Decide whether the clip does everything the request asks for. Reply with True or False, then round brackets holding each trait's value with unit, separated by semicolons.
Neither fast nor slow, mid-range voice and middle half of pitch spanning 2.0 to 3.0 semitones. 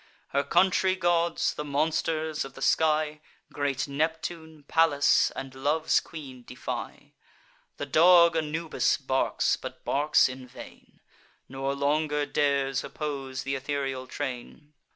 False (120 wpm; 145 Hz; 2.7 semitones)